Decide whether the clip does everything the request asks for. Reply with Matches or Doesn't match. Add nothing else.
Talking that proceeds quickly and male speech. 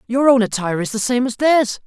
Matches